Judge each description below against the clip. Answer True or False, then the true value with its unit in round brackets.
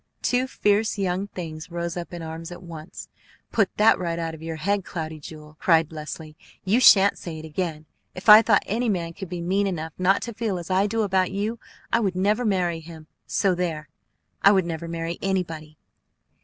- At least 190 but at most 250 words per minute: True (200 wpm)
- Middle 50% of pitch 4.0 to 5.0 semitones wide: False (3.5 semitones)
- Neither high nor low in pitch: True (180 Hz)